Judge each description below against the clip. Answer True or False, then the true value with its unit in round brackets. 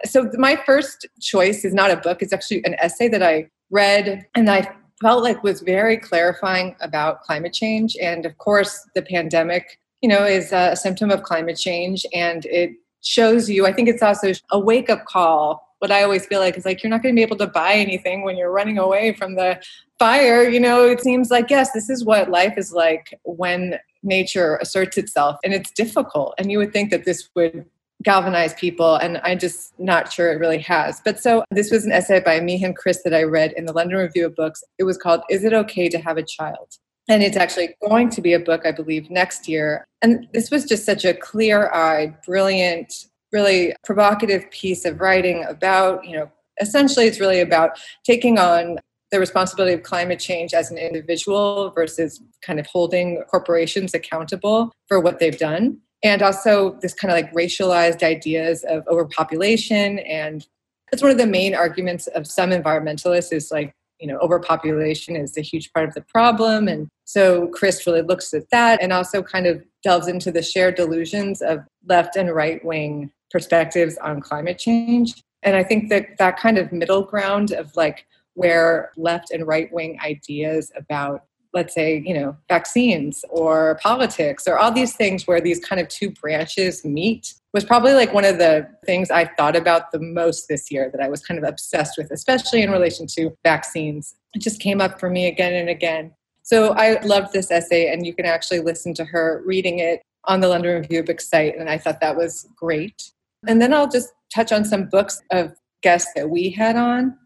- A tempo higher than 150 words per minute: True (200 wpm)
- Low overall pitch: False (180 Hz)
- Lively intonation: False (3.5 semitones)